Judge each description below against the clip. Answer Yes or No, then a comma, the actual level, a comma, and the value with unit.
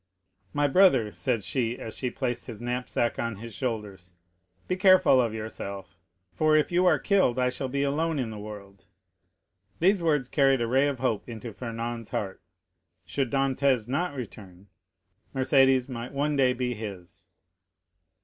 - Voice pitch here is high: No, low, 125 Hz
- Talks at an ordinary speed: Yes, average, 160 wpm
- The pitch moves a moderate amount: Yes, average, 3.9 semitones